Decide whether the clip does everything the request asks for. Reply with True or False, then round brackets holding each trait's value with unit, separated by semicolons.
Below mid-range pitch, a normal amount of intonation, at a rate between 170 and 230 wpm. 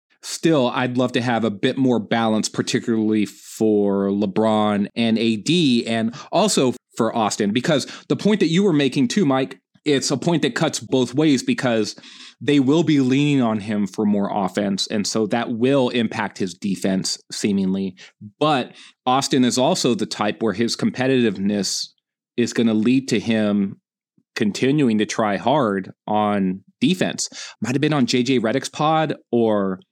False (115 Hz; 4.0 semitones; 160 wpm)